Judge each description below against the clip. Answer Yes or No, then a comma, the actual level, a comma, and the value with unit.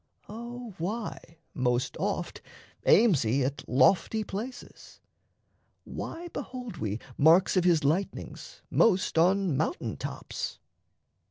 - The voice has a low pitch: No, medium, 185 Hz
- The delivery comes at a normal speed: No, slow, 105 wpm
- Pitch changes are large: Yes, wide, 8.0 semitones